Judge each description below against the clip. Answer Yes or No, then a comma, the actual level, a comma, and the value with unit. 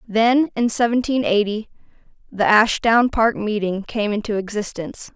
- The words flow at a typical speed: No, slow, 130 wpm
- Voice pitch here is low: No, high, 220 Hz